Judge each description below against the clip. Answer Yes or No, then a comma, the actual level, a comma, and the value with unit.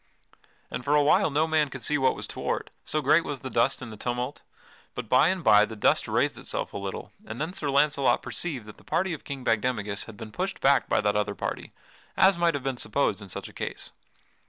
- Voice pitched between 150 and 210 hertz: No, low, 135 Hz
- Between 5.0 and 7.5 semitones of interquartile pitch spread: Yes, wide, 5.4 semitones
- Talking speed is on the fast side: Yes, fast, 235 wpm